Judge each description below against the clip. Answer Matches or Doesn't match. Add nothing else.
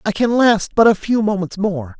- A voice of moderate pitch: Doesn't match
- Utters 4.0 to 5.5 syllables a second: Matches